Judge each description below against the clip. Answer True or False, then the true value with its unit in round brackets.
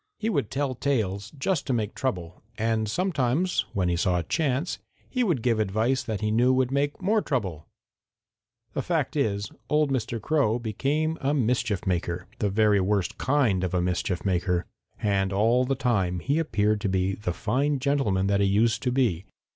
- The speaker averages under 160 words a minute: False (185 wpm)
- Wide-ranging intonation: True (5.9 semitones)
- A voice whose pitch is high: False (110 Hz)